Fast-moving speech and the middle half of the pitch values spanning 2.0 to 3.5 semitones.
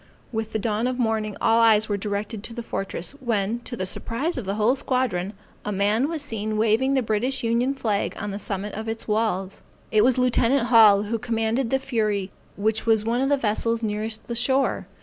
Yes: fast, 210 wpm; average, 2.7 semitones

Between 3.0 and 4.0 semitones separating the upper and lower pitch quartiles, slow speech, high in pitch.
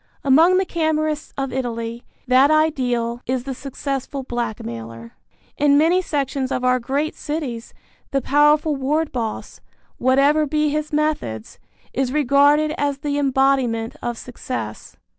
Yes: average, 3.6 semitones; slow, 130 wpm; very high, 275 Hz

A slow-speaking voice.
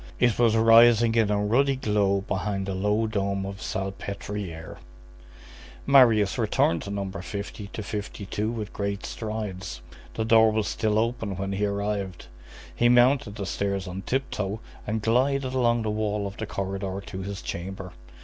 No: average, 160 wpm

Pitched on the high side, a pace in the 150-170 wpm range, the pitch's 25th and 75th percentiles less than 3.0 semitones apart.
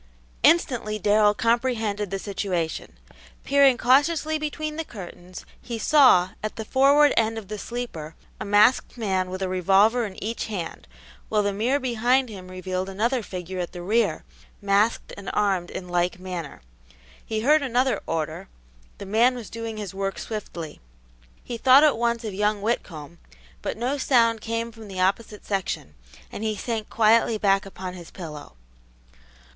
No: high, 215 Hz; average, 160 wpm; average, 4.0 semitones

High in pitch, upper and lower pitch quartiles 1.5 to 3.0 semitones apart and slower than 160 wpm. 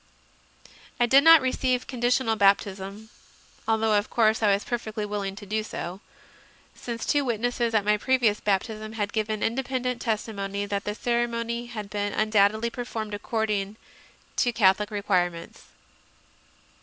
Yes: high, 220 Hz; narrow, 2.6 semitones; average, 145 wpm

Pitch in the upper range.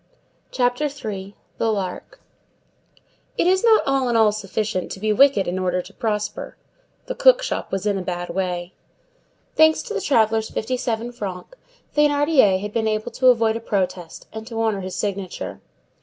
Yes: high, 220 Hz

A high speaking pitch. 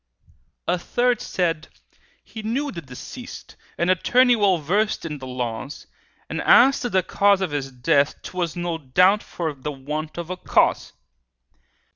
No: medium, 175 Hz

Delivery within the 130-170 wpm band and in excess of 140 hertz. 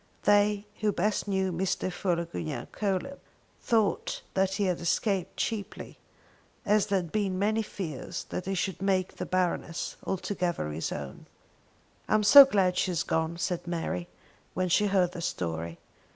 Yes: average, 155 wpm; medium, 185 Hz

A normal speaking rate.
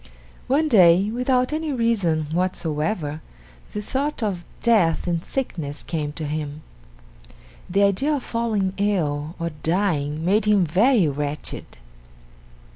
No: slow, 120 wpm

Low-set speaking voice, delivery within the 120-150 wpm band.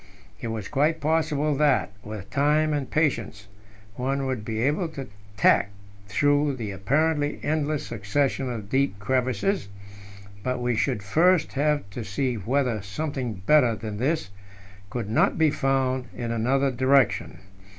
Yes: low, 130 Hz; average, 140 wpm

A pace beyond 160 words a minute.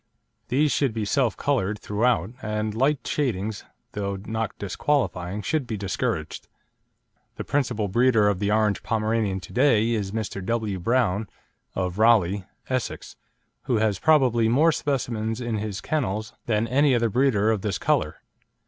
No: average, 150 wpm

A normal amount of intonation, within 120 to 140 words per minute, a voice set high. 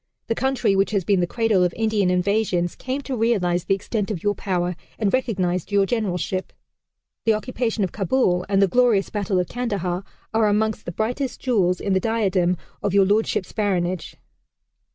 No: average, 3.5 semitones; average, 175 wpm; high, 200 Hz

